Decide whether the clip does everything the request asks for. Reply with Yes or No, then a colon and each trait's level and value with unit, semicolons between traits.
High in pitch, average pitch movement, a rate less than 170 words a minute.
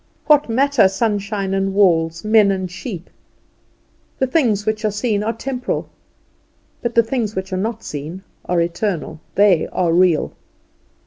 Yes: high, 200 Hz; average, 3.6 semitones; average, 145 wpm